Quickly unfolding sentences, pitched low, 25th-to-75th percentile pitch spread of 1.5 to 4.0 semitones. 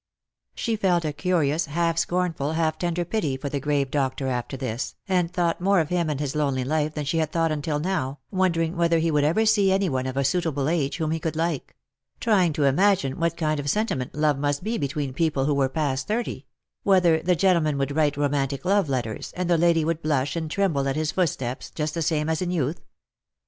No: fast, 220 wpm; medium, 155 Hz; average, 3.5 semitones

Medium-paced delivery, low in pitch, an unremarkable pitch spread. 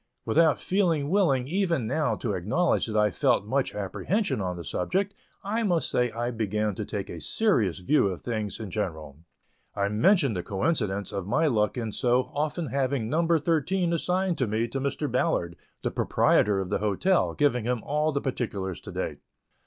No: average, 185 wpm; low, 125 Hz; wide, 7.6 semitones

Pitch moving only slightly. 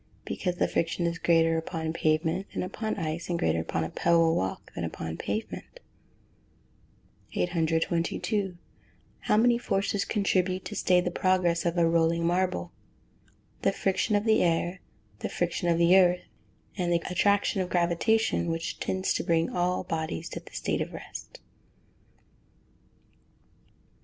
Yes: narrow, 2.2 semitones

